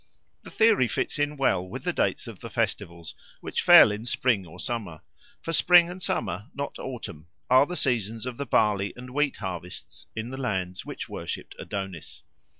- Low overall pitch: Yes, low, 115 Hz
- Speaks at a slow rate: No, average, 180 wpm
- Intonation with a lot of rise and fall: Yes, wide, 6.4 semitones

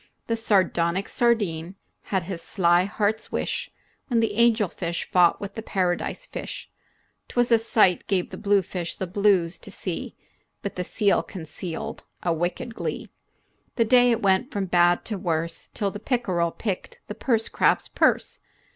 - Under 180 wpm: Yes, average, 160 wpm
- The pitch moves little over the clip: No, average, 4.2 semitones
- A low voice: No, high, 195 Hz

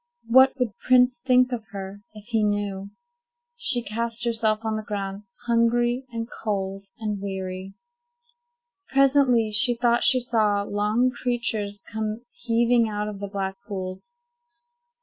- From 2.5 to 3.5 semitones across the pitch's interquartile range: Yes, average, 3.0 semitones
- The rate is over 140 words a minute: No, slow, 135 wpm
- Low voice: No, high, 220 Hz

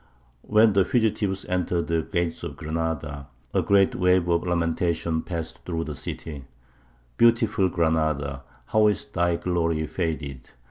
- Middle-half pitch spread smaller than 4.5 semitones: Yes, average, 2.8 semitones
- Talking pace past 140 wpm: No, slow, 135 wpm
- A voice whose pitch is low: Yes, very low, 85 Hz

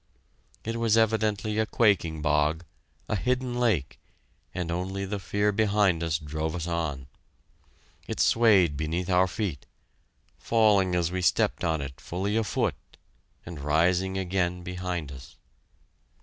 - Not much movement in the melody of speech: No, average, 4.4 semitones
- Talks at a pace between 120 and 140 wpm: Yes, slow, 135 wpm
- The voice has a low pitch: Yes, very low, 90 Hz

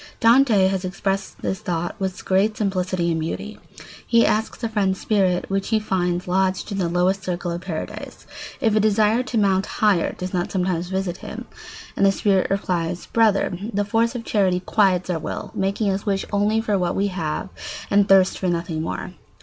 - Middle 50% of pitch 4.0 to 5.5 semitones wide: No, narrow, 2.5 semitones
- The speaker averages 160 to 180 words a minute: No, average, 190 wpm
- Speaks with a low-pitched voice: No, high, 195 Hz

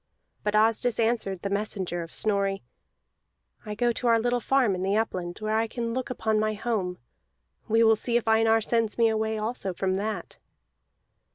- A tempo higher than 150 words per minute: Yes, average, 180 wpm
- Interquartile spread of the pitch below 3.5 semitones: Yes, narrow, 2.4 semitones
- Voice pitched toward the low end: No, high, 220 Hz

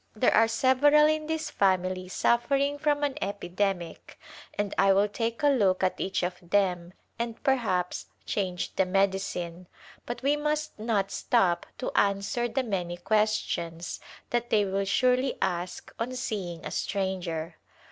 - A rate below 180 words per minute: Yes, average, 145 wpm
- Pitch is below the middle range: No, high, 200 Hz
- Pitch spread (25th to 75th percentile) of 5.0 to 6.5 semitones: Yes, average, 5.3 semitones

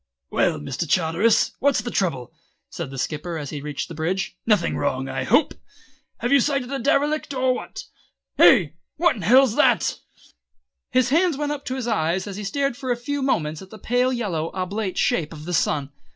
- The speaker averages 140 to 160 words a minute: No, average, 195 wpm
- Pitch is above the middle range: Yes, high, 205 Hz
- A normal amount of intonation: No, wide, 8.4 semitones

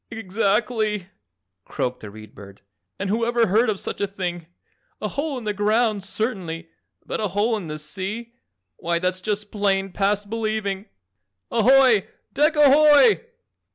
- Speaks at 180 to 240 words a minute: No, average, 145 wpm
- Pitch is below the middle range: No, high, 210 Hz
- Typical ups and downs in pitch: Yes, average, 3.6 semitones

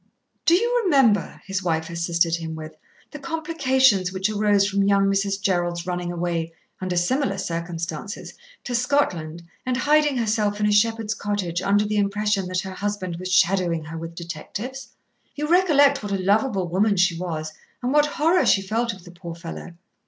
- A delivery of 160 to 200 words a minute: Yes, average, 175 wpm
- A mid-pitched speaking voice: No, high, 195 Hz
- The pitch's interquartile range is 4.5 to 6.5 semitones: Yes, average, 5.1 semitones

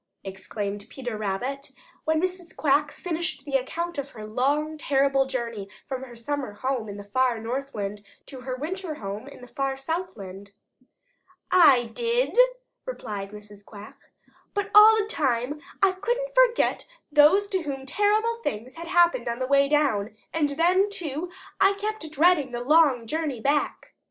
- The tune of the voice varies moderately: No, wide, 6.5 semitones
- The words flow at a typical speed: Yes, average, 155 wpm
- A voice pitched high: Yes, very high, 275 Hz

